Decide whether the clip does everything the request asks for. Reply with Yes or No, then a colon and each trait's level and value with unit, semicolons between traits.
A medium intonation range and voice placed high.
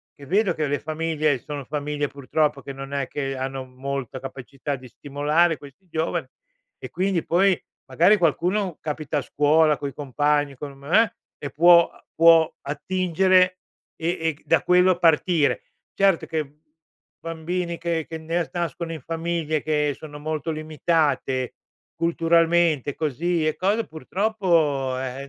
No: average, 3.0 semitones; medium, 155 Hz